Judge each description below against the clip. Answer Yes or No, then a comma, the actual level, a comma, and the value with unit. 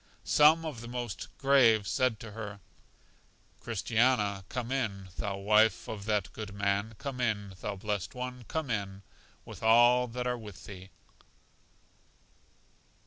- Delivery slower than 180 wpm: Yes, average, 140 wpm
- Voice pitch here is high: No, low, 110 Hz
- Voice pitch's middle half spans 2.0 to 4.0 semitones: Yes, average, 3.6 semitones